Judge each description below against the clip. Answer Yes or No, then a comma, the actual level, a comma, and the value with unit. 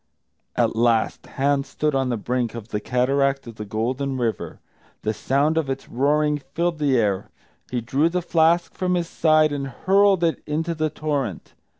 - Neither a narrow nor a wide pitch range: Yes, average, 4.4 semitones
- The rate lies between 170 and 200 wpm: Yes, average, 180 wpm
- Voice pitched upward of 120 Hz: Yes, medium, 140 Hz